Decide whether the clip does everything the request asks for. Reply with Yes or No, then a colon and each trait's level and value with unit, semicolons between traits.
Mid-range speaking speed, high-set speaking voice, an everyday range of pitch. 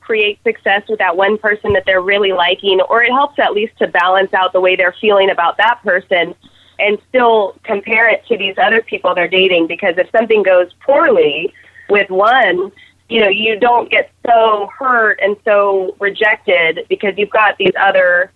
Yes: average, 185 wpm; high, 205 Hz; average, 3.7 semitones